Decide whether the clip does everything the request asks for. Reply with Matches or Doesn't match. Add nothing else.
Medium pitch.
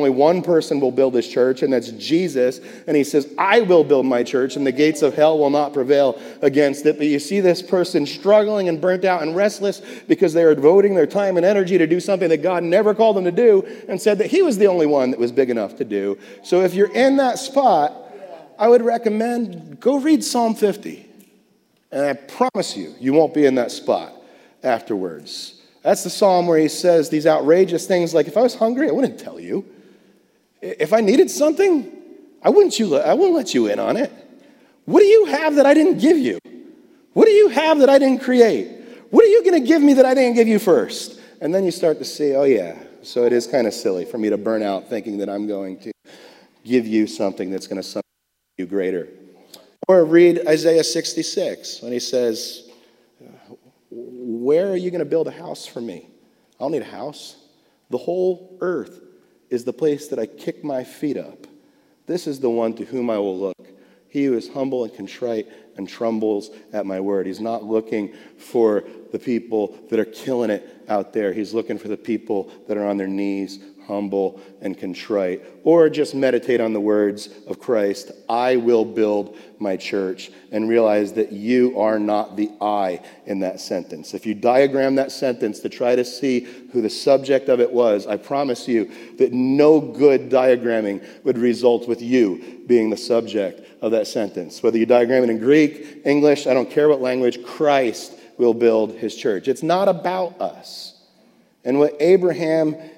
Matches